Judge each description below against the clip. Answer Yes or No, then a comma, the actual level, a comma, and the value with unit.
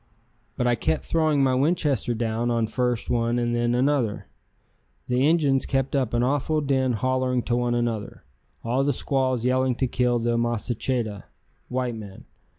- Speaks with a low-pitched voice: Yes, low, 125 Hz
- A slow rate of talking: No, average, 160 wpm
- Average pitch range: No, narrow, 2.1 semitones